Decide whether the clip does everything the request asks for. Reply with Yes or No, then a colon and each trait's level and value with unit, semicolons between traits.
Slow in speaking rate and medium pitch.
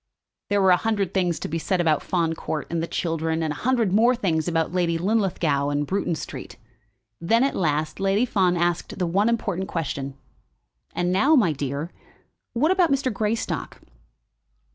No: average, 175 wpm; medium, 180 Hz